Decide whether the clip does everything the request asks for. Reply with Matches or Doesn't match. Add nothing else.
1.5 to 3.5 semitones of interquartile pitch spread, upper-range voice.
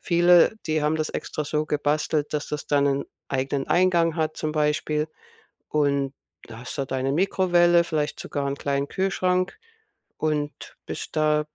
Doesn't match